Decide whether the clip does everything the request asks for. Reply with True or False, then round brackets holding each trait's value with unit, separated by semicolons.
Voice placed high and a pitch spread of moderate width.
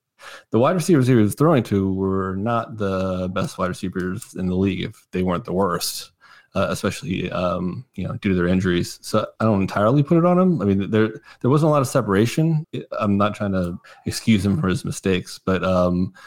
False (100 Hz; 4.2 semitones)